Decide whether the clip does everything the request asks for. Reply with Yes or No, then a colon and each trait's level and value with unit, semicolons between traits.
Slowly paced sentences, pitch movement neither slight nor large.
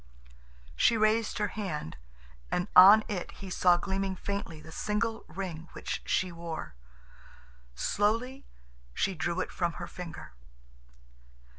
Yes: slow, 125 wpm; average, 3.5 semitones